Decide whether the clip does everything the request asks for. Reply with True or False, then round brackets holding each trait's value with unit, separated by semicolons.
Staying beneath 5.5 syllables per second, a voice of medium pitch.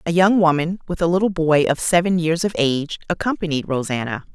False (5.8 syllables/s; 165 Hz)